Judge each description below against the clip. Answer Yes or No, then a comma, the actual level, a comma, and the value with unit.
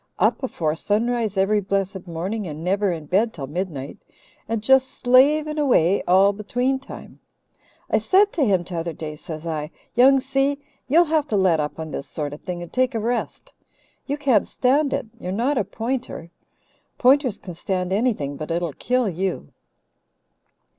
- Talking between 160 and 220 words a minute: Yes, average, 170 wpm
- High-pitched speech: Yes, high, 205 Hz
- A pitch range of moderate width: No, wide, 7.1 semitones